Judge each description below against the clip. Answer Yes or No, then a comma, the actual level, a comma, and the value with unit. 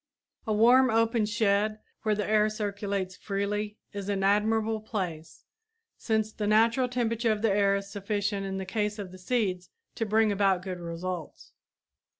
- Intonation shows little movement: Yes, narrow, 1.9 semitones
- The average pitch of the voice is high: Yes, high, 210 Hz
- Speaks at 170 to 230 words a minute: No, average, 155 wpm